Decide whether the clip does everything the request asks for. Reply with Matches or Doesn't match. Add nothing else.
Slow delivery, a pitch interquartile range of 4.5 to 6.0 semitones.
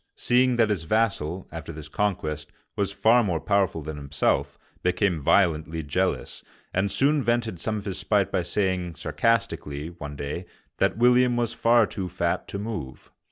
Doesn't match